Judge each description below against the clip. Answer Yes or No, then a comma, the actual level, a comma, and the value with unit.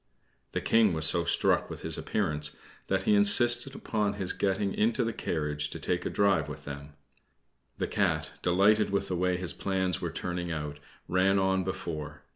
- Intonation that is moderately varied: Yes, average, 4.3 semitones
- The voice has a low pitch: Yes, very low, 90 Hz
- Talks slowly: No, average, 180 wpm